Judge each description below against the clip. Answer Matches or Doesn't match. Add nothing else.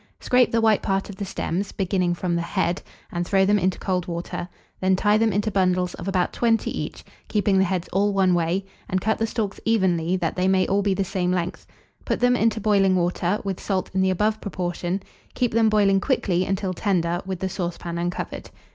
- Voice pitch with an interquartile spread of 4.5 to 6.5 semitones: Doesn't match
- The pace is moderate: Doesn't match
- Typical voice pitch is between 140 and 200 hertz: Matches